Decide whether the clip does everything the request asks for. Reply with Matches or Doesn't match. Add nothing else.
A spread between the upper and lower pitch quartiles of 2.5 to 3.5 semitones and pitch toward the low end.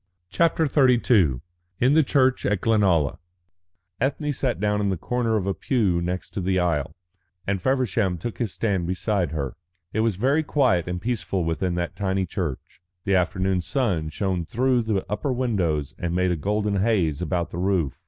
Doesn't match